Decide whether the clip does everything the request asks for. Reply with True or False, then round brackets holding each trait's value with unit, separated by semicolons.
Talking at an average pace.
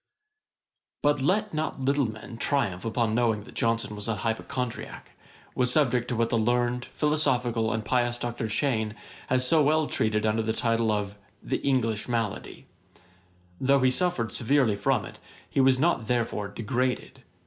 True (160 wpm)